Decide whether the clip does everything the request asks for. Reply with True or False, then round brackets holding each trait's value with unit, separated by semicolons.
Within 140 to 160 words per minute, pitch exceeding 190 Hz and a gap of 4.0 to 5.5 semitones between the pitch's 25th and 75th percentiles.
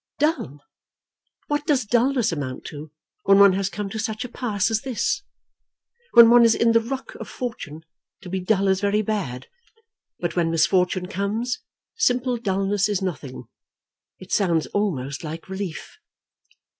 True (155 wpm; 200 Hz; 4.6 semitones)